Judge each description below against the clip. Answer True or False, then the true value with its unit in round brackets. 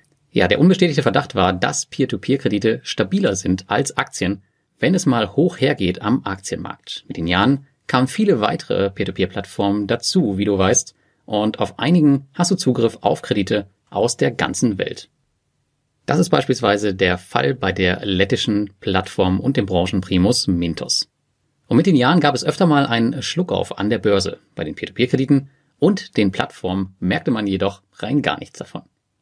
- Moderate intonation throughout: False (6.3 semitones)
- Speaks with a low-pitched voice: True (105 Hz)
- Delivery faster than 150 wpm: True (160 wpm)